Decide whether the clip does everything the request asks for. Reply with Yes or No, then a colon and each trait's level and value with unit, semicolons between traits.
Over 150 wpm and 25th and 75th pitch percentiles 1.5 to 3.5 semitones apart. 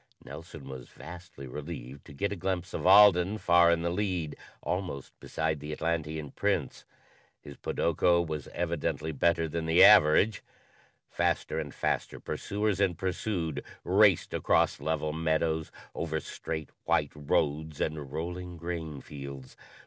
No: slow, 135 wpm; average, 2.7 semitones